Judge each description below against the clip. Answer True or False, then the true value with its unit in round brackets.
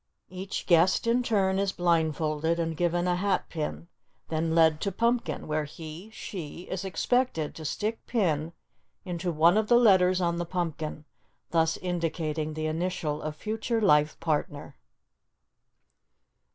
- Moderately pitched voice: True (170 Hz)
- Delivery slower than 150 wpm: True (140 wpm)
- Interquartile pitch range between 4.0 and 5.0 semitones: False (3.4 semitones)